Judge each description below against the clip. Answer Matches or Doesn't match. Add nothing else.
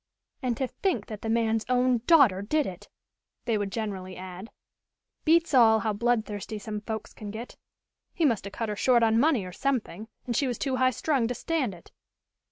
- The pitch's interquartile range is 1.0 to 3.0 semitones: Doesn't match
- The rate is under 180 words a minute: Doesn't match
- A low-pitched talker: Doesn't match